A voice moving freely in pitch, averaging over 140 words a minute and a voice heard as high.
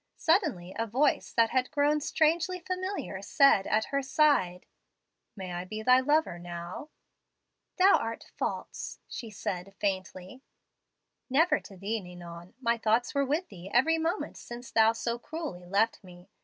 Yes: wide, 8.0 semitones; average, 150 wpm; high, 230 Hz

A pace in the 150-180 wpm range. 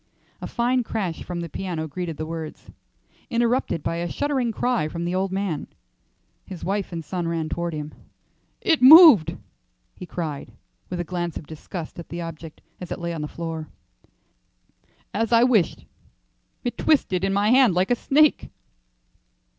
Yes: average, 165 wpm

